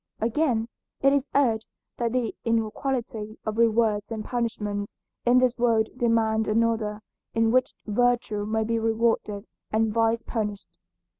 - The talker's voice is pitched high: Yes, high, 225 Hz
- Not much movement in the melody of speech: Yes, narrow, 1.6 semitones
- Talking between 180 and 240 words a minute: No, slow, 135 wpm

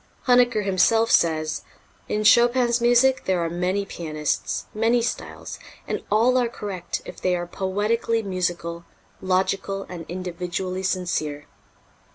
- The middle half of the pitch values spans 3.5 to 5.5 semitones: Yes, average, 4.6 semitones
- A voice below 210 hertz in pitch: Yes, high, 190 Hz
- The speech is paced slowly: Yes, slow, 125 wpm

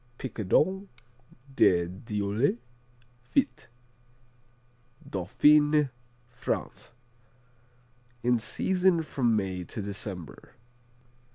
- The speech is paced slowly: Yes, slow, 65 wpm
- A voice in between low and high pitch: No, low, 120 Hz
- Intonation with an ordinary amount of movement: No, wide, 7.0 semitones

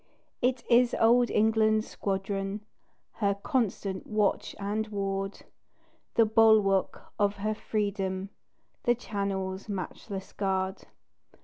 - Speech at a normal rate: No, slow, 100 wpm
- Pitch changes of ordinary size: No, narrow, 2.0 semitones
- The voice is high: Yes, high, 205 Hz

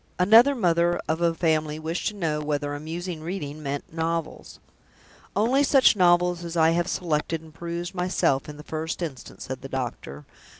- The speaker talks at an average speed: Yes, average, 170 wpm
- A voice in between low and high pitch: Yes, medium, 165 Hz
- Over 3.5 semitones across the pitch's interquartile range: No, average, 2.7 semitones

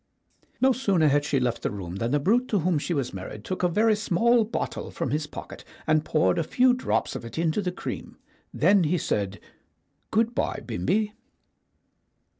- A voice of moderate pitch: Yes, medium, 170 Hz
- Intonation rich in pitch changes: Yes, wide, 6.9 semitones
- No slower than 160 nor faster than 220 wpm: Yes, average, 190 wpm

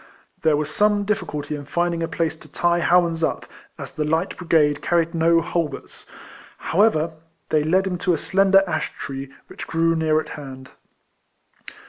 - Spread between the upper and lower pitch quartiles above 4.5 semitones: No, narrow, 2.4 semitones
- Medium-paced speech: Yes, average, 165 wpm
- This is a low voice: No, medium, 165 Hz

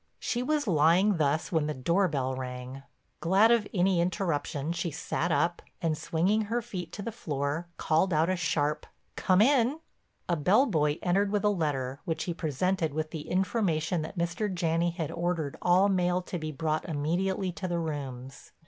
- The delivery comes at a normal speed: Yes, average, 180 wpm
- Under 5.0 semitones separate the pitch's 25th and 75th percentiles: Yes, average, 3.8 semitones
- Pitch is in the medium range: Yes, medium, 170 Hz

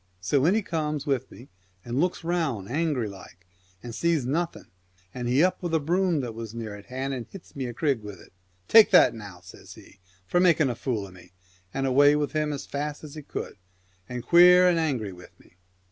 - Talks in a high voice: No, low, 135 Hz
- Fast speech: Yes, fast, 220 wpm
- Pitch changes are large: Yes, wide, 6.1 semitones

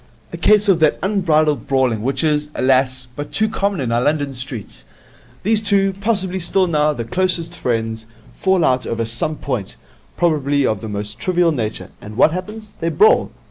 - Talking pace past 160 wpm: Yes, average, 180 wpm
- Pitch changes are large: Yes, wide, 6.8 semitones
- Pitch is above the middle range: No, medium, 150 Hz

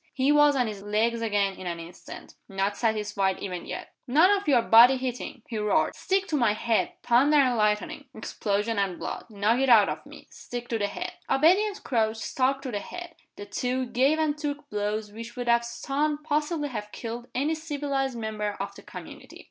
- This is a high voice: Yes, high, 240 Hz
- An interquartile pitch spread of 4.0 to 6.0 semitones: Yes, wide, 5.4 semitones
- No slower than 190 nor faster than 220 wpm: Yes, average, 195 wpm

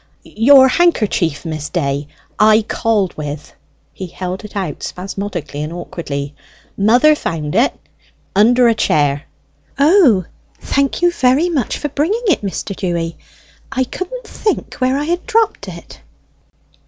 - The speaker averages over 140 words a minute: No, slow, 135 wpm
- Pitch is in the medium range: No, high, 210 Hz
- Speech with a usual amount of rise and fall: No, wide, 8.7 semitones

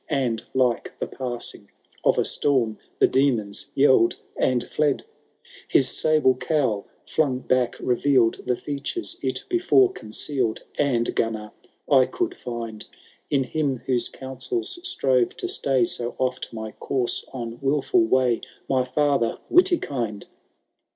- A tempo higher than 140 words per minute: No, slow, 135 wpm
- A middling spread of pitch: Yes, average, 3.3 semitones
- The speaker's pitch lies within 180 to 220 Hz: No, low, 130 Hz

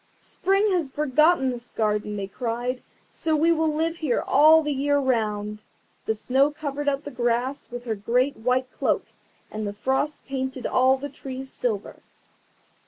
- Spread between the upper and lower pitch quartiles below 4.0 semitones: Yes, average, 3.6 semitones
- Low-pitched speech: No, very high, 265 Hz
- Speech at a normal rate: Yes, average, 165 wpm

